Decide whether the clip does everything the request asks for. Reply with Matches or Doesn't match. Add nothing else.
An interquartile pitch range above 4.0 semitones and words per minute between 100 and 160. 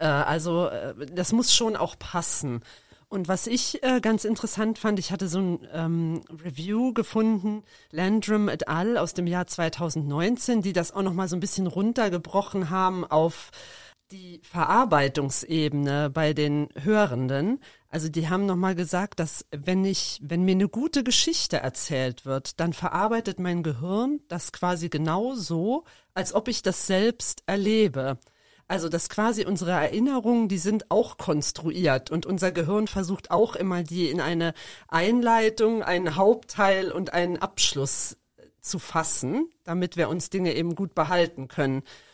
Matches